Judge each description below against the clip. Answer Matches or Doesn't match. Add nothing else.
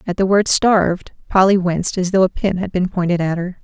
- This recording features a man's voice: Doesn't match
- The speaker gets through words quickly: Matches